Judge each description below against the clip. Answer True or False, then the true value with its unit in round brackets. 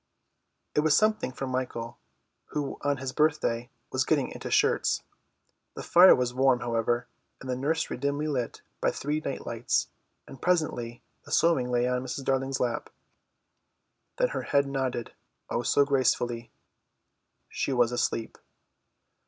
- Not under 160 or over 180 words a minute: False (145 wpm)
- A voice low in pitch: True (130 Hz)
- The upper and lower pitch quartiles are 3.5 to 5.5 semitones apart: False (2.8 semitones)